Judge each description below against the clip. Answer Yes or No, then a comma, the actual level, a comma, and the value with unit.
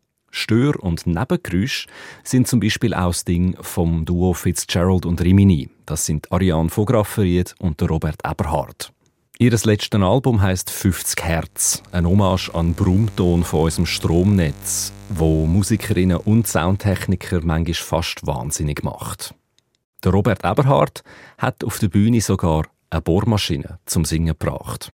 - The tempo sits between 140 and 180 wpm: No, average, 130 wpm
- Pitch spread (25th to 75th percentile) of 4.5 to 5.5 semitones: No, average, 3.6 semitones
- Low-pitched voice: Yes, very low, 90 Hz